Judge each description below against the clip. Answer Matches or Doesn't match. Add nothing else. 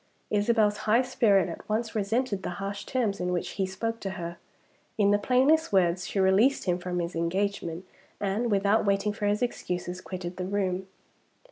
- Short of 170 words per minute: Doesn't match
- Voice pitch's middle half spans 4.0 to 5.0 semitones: Doesn't match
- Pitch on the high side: Matches